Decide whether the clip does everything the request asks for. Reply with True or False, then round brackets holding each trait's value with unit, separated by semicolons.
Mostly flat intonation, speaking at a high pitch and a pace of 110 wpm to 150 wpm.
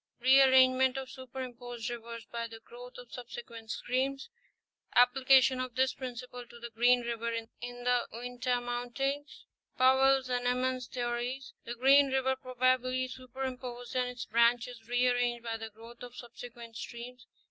True (1.3 semitones; 245 Hz; 145 wpm)